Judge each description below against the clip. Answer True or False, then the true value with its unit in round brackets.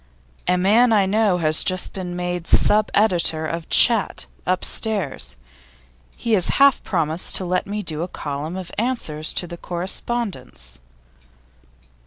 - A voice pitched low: False (180 Hz)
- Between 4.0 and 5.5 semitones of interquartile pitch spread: True (4.3 semitones)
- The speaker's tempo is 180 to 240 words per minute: False (135 wpm)